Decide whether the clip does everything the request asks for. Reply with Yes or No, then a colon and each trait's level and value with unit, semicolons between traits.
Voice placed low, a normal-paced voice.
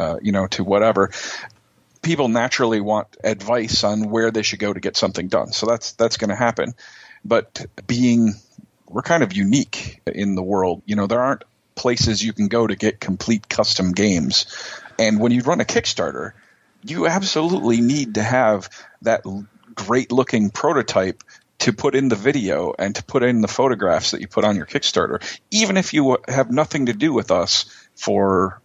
Yes: low, 115 Hz; average, 190 wpm